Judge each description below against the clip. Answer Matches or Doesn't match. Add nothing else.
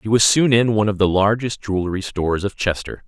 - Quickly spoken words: Matches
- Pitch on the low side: Matches